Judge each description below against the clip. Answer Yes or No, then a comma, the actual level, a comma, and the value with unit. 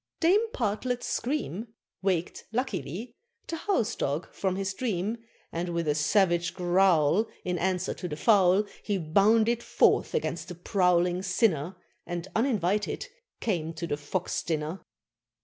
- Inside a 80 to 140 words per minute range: Yes, slow, 135 wpm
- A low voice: No, medium, 185 Hz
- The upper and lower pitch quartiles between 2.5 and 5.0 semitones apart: Yes, average, 4.4 semitones